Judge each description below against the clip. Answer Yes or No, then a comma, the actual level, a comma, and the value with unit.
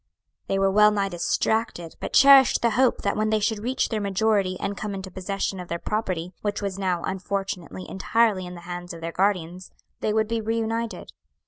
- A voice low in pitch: No, high, 200 Hz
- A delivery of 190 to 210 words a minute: Yes, average, 200 wpm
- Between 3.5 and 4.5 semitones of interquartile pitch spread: No, average, 3.1 semitones